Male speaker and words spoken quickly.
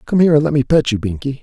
Yes: male; fast, 335 wpm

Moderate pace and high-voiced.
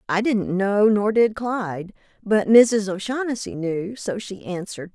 Yes: average, 160 wpm; high, 205 Hz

